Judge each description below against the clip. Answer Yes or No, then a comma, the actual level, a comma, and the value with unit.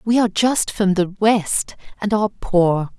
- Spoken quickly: No, average, 180 wpm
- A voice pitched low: No, high, 200 Hz